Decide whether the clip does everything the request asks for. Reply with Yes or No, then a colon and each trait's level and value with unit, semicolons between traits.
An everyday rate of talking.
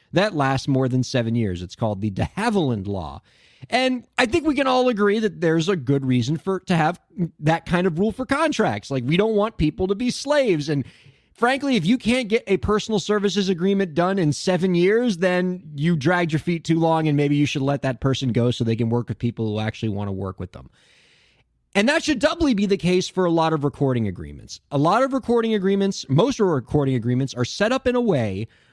No: fast, 230 wpm